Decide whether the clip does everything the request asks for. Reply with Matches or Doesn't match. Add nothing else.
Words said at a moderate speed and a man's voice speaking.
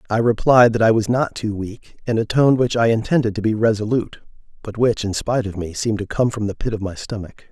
Doesn't match